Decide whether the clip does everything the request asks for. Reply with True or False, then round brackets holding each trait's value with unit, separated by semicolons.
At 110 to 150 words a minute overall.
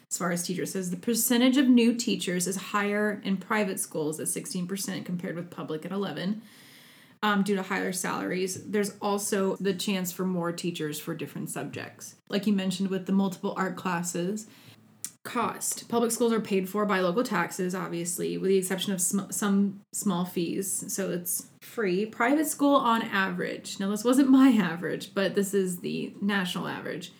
False (180 wpm)